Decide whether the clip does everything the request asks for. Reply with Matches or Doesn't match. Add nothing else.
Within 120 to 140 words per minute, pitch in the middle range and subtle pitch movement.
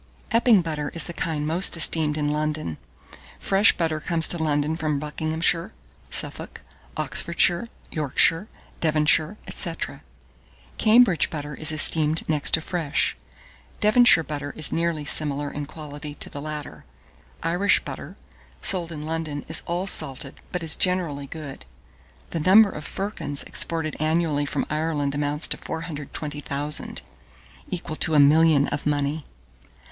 Matches